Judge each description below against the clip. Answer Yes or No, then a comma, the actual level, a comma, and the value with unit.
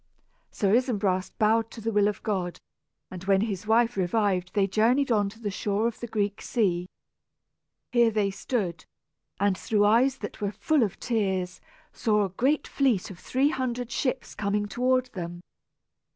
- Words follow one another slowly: No, average, 165 wpm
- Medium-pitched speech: No, high, 210 Hz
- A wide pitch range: No, average, 3.3 semitones